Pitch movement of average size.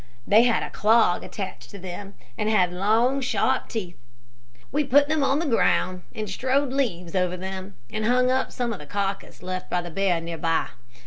No: wide, 5.7 semitones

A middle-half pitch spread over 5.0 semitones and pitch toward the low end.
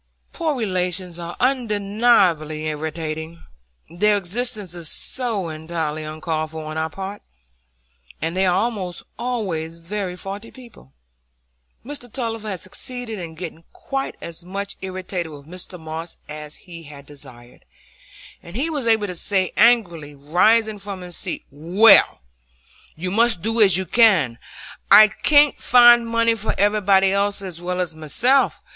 No: wide, 5.4 semitones; medium, 185 Hz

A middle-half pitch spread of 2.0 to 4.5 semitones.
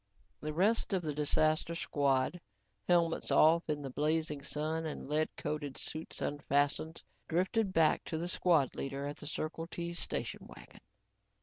Yes: narrow, 2.4 semitones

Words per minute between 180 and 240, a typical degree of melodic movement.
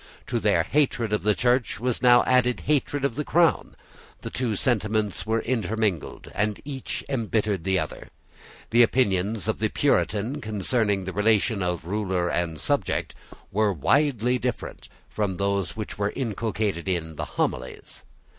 No: average, 150 wpm; average, 4.2 semitones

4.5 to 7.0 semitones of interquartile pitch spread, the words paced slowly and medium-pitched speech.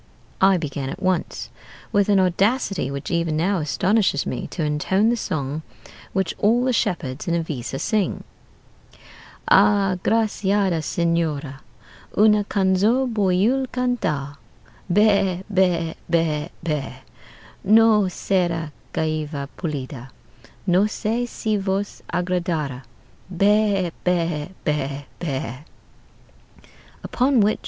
Yes: average, 5.1 semitones; slow, 100 wpm; medium, 180 Hz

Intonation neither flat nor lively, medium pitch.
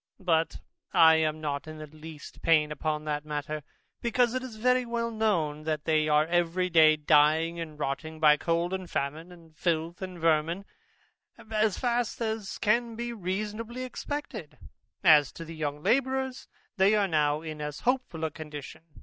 No: wide, 6.0 semitones; medium, 165 Hz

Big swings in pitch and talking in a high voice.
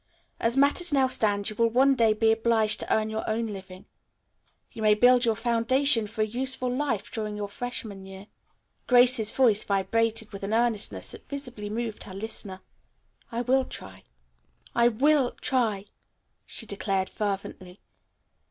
No: average, 3.1 semitones; high, 225 Hz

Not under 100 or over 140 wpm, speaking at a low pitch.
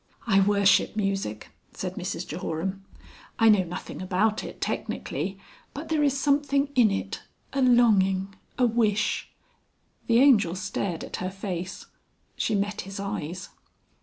No: slow, 135 wpm; high, 200 Hz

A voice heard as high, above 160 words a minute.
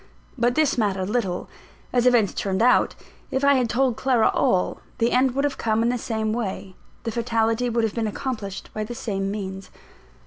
Yes: high, 230 Hz; average, 195 wpm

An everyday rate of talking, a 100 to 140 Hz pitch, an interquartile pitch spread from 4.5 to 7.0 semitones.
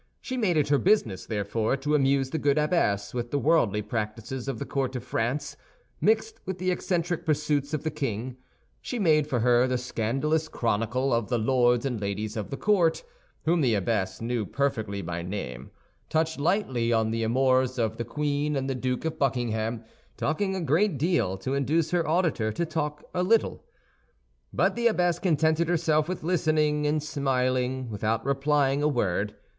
Yes: average, 180 wpm; low, 135 Hz; average, 5.3 semitones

